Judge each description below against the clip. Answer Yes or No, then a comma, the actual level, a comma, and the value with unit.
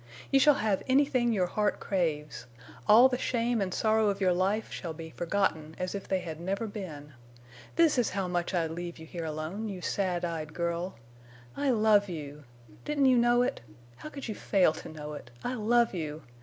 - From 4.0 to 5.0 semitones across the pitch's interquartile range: No, wide, 5.6 semitones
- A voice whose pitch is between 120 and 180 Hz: No, high, 190 Hz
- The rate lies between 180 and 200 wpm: Yes, average, 190 wpm